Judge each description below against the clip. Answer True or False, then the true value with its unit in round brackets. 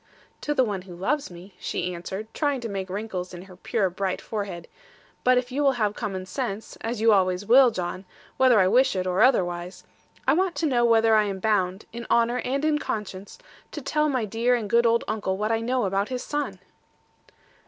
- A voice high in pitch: True (215 Hz)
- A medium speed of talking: False (210 wpm)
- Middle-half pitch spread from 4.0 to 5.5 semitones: True (4.7 semitones)